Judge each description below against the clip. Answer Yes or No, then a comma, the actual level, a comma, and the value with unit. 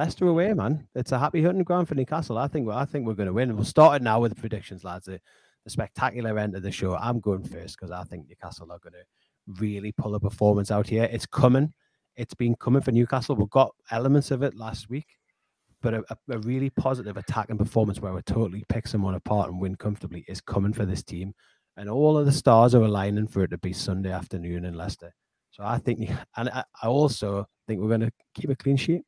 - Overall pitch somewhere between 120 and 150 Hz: No, low, 110 Hz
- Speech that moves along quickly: Yes, fast, 240 wpm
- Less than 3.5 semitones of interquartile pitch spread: No, average, 4.9 semitones